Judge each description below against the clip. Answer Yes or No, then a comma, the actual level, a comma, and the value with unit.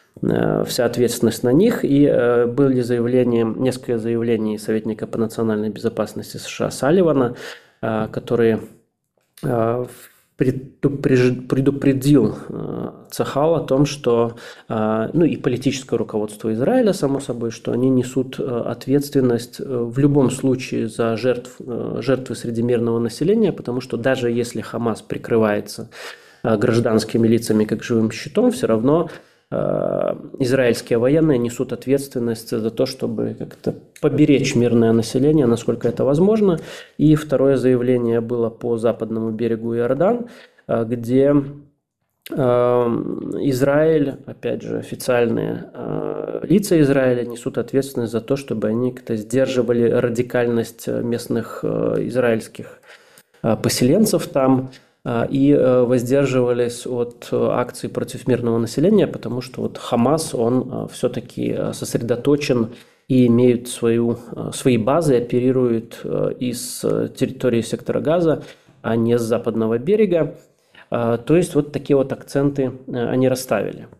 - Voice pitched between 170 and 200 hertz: No, low, 125 Hz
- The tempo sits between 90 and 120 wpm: Yes, slow, 110 wpm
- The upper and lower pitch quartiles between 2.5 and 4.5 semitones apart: Yes, average, 2.9 semitones